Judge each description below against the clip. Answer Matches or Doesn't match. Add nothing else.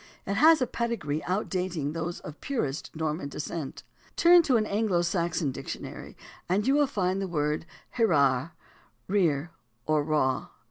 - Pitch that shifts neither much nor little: Doesn't match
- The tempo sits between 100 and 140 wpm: Doesn't match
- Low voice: Doesn't match